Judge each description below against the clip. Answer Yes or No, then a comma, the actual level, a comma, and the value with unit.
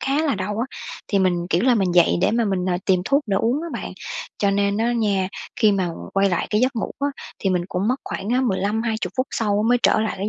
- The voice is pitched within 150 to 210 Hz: Yes, high, 205 Hz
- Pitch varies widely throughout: No, average, 3.9 semitones